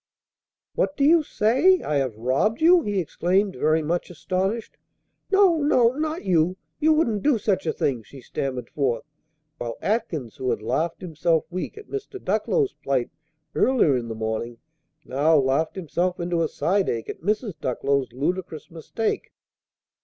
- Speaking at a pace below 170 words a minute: Yes, average, 160 wpm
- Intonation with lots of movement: Yes, wide, 8.9 semitones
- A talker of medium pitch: Yes, medium, 175 Hz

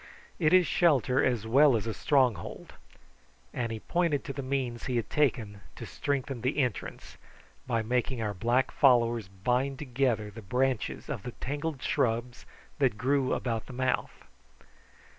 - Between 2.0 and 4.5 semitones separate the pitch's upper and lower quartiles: Yes, average, 3.1 semitones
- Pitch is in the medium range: No, low, 125 Hz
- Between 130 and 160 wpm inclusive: Yes, average, 155 wpm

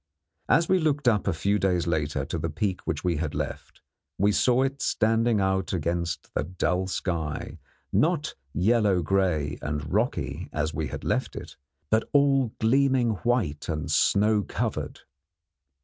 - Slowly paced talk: No, average, 155 wpm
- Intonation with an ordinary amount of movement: No, wide, 6.4 semitones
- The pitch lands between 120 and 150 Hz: No, very low, 95 Hz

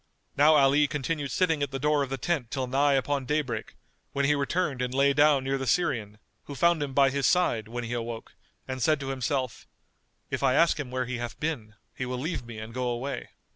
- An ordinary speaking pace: No, fast, 225 wpm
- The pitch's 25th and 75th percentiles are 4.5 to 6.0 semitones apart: No, average, 2.8 semitones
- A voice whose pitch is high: No, low, 135 Hz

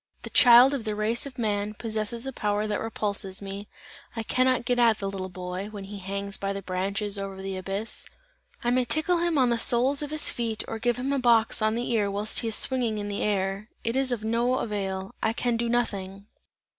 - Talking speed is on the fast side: Yes, fast, 225 wpm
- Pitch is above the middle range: Yes, high, 215 Hz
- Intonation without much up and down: No, average, 3.4 semitones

